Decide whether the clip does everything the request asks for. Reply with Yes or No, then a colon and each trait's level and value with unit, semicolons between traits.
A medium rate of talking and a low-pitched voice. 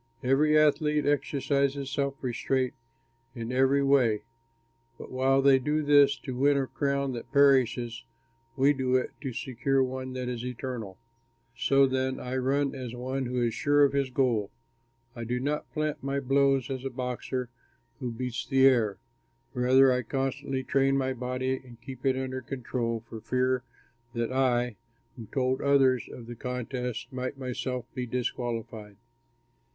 Yes: average, 155 wpm; low, 130 Hz